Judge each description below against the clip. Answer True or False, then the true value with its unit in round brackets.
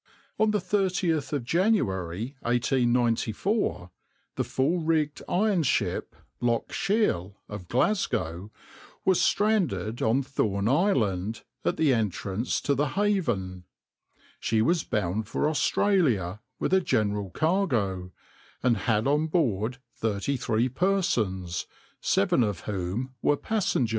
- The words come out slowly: True (120 wpm)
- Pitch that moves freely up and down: True (8.7 semitones)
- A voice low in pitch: True (125 Hz)